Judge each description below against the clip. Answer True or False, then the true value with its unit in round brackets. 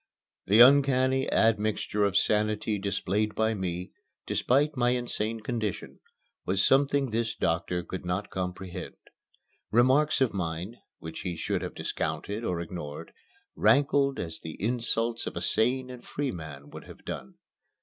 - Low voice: True (110 Hz)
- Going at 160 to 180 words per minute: False (140 wpm)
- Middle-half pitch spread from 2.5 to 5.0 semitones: False (5.6 semitones)